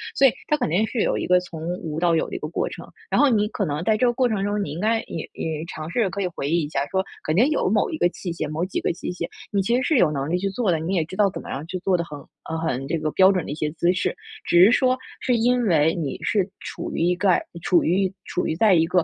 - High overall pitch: No, medium, 180 Hz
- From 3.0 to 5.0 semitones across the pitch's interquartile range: Yes, average, 4.6 semitones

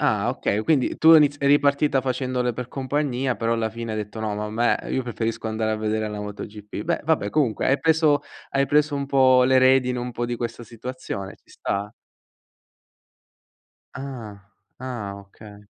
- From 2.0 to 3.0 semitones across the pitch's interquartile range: No, average, 4.0 semitones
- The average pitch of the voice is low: Yes, low, 120 Hz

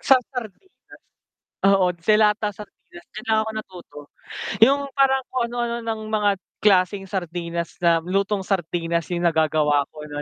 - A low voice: No, high, 195 Hz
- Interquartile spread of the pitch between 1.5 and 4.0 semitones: No, average, 4.4 semitones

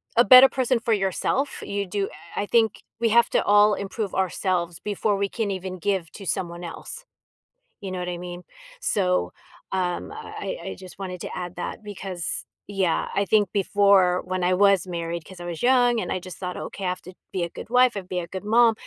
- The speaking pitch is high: Yes, high, 195 Hz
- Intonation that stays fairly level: No, average, 3.1 semitones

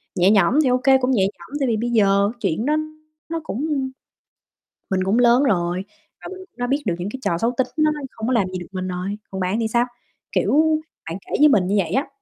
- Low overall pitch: No, high, 225 Hz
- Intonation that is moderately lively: No, wide, 5.7 semitones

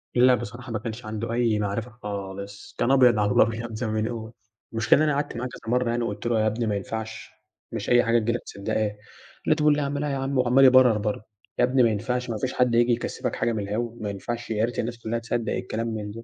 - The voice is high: No, low, 115 Hz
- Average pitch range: No, narrow, 2.3 semitones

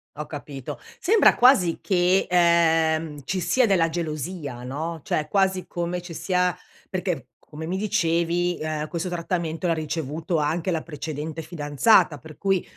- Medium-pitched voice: Yes, medium, 165 Hz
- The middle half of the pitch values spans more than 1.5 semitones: Yes, narrow, 2.6 semitones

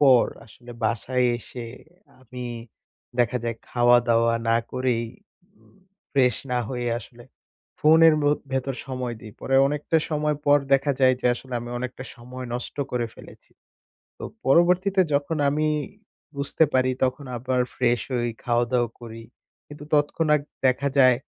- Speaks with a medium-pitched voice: No, low, 130 Hz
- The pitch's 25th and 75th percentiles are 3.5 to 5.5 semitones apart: No, average, 2.8 semitones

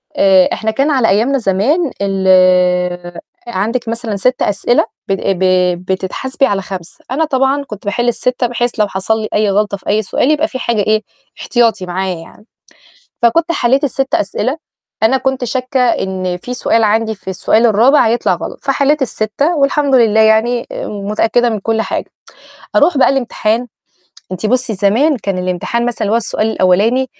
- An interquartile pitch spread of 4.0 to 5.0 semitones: Yes, average, 4.6 semitones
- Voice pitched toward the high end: Yes, high, 225 Hz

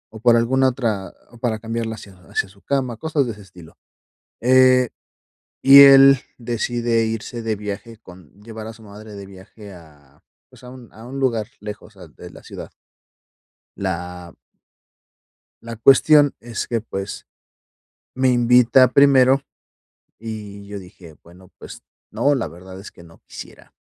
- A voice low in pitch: Yes, low, 115 Hz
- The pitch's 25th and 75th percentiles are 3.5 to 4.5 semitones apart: Yes, average, 4.1 semitones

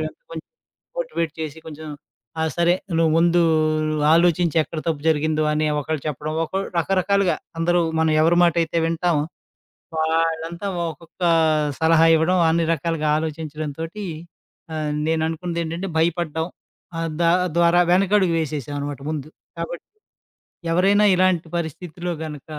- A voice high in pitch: No, medium, 165 Hz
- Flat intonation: Yes, narrow, 1.9 semitones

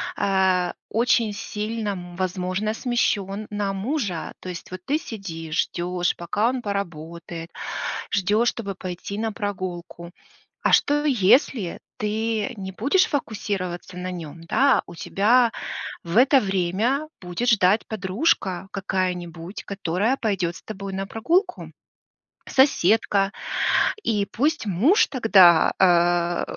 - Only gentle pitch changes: No, average, 4.0 semitones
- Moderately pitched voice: No, high, 195 Hz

